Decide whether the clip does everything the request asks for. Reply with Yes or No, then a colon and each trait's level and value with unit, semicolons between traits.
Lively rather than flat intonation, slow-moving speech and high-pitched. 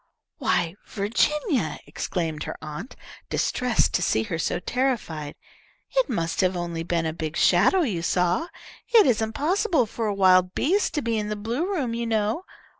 No: wide, 7.4 semitones; average, 170 wpm; high, 210 Hz